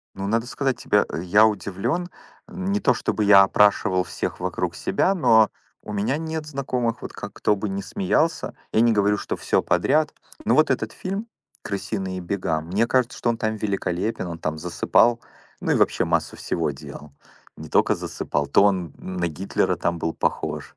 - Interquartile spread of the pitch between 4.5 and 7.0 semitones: Yes, average, 5.2 semitones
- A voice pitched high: No, low, 105 Hz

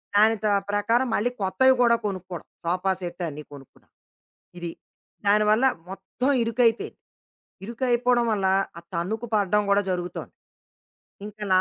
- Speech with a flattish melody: No, average, 4.0 semitones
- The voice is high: Yes, high, 205 Hz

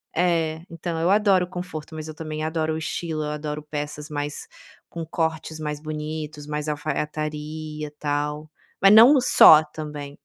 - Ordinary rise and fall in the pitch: No, narrow, 1.3 semitones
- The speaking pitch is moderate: Yes, medium, 155 Hz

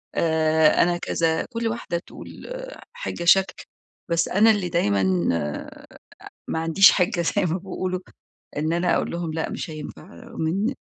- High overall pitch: No, medium, 170 Hz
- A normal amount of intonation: Yes, average, 3.2 semitones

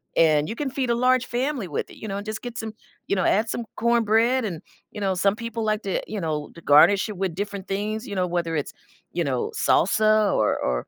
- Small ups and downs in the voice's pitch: No, average, 4.5 semitones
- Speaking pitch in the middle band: No, high, 205 Hz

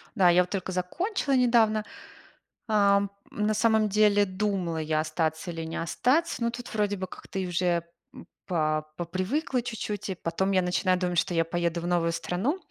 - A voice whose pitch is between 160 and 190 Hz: Yes, medium, 185 Hz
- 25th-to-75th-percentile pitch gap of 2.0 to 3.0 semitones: No, average, 3.8 semitones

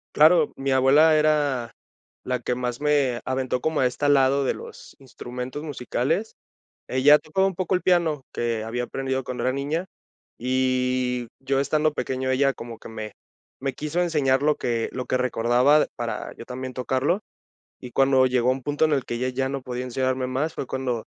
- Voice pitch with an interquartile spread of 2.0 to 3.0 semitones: Yes, average, 2.7 semitones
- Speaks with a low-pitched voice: Yes, low, 130 Hz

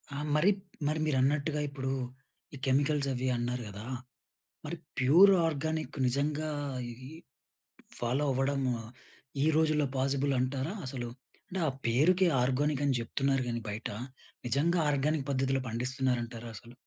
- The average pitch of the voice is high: No, low, 135 Hz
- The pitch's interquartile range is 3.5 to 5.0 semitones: No, average, 3.0 semitones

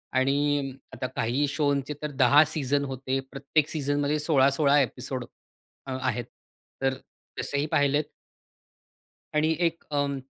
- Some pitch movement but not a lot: No, narrow, 1.6 semitones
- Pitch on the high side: No, medium, 140 Hz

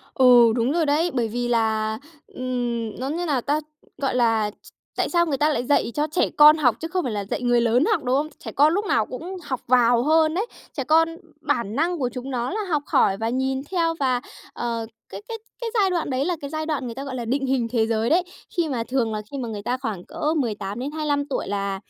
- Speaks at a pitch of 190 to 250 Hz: No, very high, 260 Hz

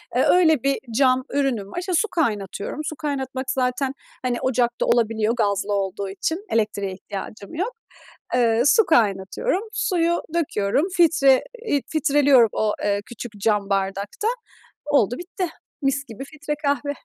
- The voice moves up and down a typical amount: No, wide, 6.1 semitones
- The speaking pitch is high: Yes, very high, 255 Hz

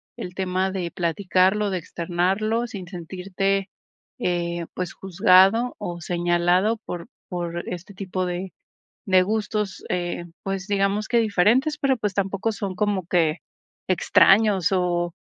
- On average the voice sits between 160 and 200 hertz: Yes, high, 190 Hz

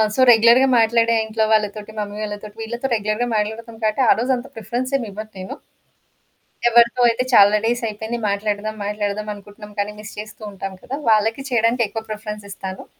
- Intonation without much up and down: Yes, narrow, 1.9 semitones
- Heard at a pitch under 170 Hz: No, high, 215 Hz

